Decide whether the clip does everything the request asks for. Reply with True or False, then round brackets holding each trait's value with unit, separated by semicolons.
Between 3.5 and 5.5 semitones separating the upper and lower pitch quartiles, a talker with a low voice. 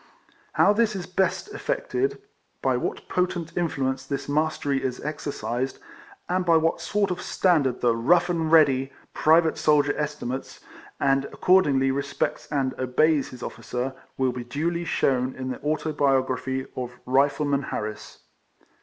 False (4.0 semitones; 145 Hz)